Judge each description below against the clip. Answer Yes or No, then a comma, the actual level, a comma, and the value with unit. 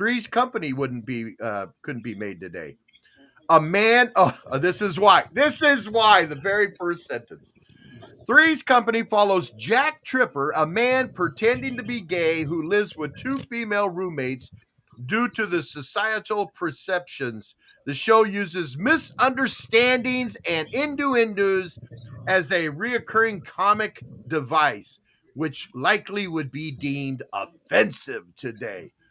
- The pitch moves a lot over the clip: Yes, wide, 7.4 semitones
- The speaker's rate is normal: No, slow, 130 wpm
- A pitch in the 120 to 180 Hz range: No, high, 195 Hz